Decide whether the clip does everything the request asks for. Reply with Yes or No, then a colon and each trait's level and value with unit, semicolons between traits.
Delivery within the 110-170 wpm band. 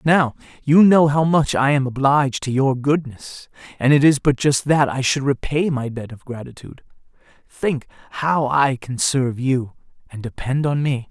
No: average, 185 wpm